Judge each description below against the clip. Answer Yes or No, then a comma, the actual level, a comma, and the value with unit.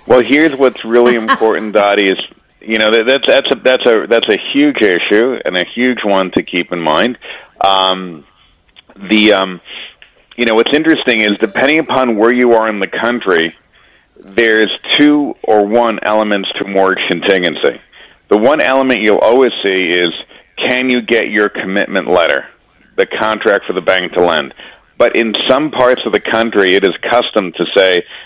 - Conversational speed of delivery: Yes, average, 175 wpm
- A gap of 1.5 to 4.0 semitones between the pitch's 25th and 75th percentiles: No, average, 4.4 semitones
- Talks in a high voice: No, low, 110 Hz